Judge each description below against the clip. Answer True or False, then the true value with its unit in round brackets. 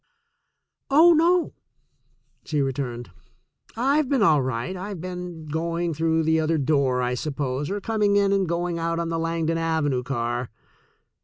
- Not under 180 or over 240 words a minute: False (155 wpm)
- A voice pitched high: False (165 Hz)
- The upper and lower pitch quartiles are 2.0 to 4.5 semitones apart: False (5.0 semitones)